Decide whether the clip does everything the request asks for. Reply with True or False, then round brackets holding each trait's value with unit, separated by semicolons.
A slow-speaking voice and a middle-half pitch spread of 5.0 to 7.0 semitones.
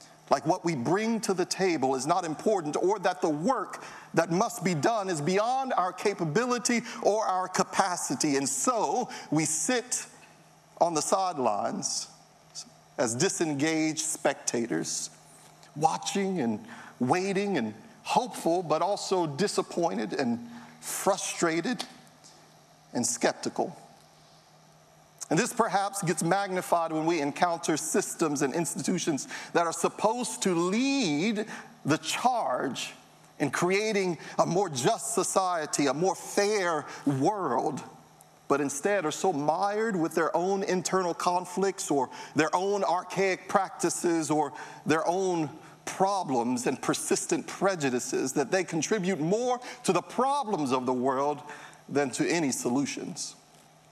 False (125 wpm; 4.2 semitones)